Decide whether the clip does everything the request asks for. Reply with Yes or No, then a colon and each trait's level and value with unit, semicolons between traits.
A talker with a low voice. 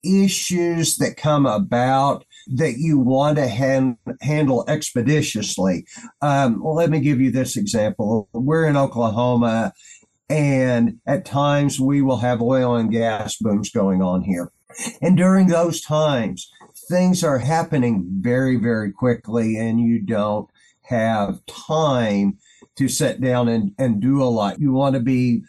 Yes: low, 130 Hz